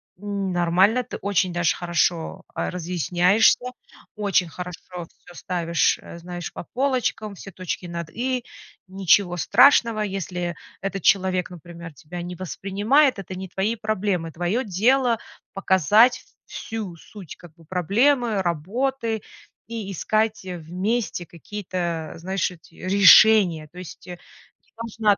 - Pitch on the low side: No, high, 190 Hz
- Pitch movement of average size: Yes, average, 3.6 semitones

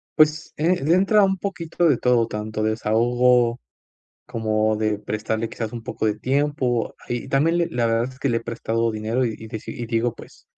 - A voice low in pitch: Yes, low, 120 Hz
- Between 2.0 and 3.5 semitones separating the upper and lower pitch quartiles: No, average, 4.2 semitones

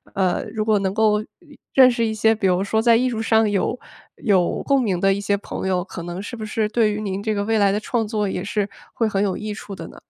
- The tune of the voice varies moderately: No, narrow, 2.2 semitones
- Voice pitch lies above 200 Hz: Yes, high, 210 Hz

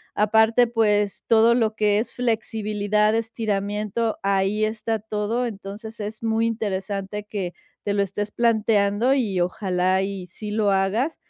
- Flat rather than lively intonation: Yes, narrow, 2.0 semitones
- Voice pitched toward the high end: Yes, high, 210 Hz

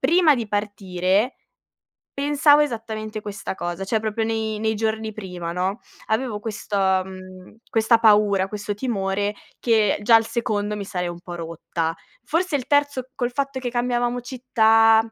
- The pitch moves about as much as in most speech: Yes, average, 3.7 semitones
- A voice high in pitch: Yes, high, 220 Hz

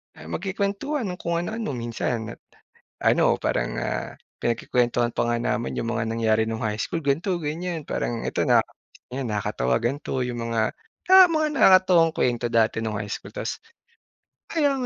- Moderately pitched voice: No, low, 125 Hz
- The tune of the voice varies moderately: No, wide, 8.4 semitones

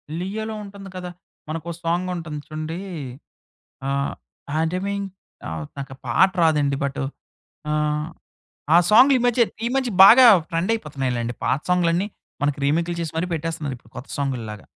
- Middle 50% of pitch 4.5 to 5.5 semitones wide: Yes, average, 5.1 semitones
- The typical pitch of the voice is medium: Yes, medium, 165 Hz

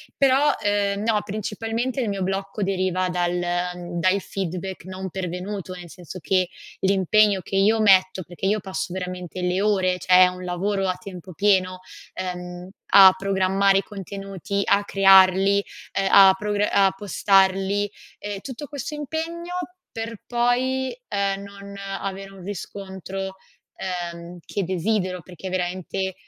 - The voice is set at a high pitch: Yes, high, 195 Hz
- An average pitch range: No, narrow, 1.8 semitones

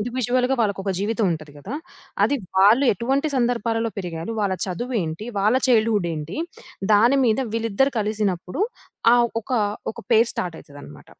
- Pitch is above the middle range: Yes, high, 215 Hz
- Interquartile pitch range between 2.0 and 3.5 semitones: No, average, 4.2 semitones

